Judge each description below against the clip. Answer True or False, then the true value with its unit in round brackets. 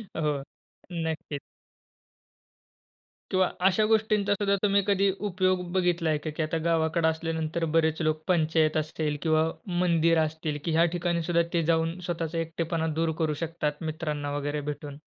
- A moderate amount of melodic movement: False (1.8 semitones)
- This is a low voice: False (165 Hz)